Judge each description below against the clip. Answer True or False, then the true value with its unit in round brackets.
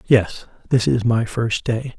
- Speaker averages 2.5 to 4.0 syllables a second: True (3.8 syllables/s)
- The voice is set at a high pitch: False (115 Hz)